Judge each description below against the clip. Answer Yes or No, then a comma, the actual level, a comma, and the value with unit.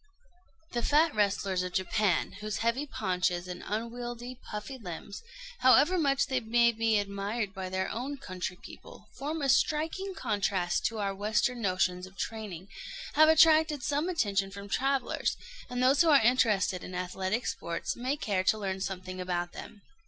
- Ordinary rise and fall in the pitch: No, wide, 5.8 semitones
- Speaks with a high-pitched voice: Yes, high, 215 Hz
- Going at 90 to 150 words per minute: No, average, 160 wpm